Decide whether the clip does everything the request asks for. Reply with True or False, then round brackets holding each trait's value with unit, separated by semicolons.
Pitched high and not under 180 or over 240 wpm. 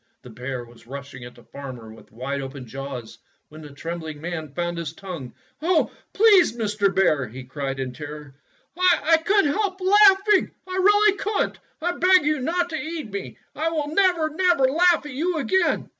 True (210 Hz; 190 wpm)